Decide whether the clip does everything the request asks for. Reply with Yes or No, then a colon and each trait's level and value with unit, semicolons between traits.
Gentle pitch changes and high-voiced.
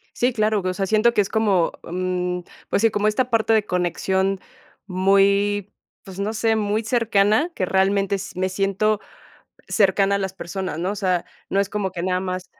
Yes: narrow, 2.3 semitones; high, 195 Hz